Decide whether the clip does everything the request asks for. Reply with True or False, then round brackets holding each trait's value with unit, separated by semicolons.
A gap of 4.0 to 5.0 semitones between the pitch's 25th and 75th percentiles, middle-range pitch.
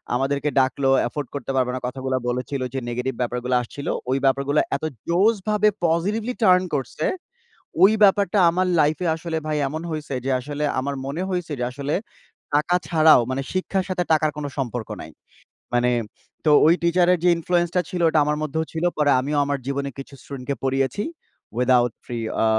True (4.4 semitones; 145 Hz)